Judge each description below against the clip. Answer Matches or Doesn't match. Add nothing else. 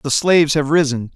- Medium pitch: Matches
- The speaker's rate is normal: Doesn't match